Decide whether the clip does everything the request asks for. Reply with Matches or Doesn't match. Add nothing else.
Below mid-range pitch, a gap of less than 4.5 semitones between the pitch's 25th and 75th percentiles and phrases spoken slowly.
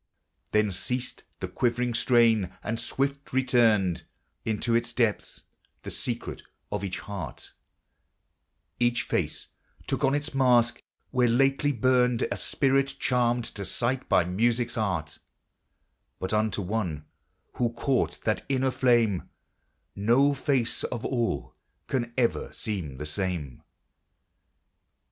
Matches